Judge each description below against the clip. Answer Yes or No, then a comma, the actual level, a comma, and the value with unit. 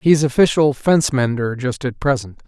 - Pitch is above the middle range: No, low, 135 Hz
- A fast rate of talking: No, average, 170 wpm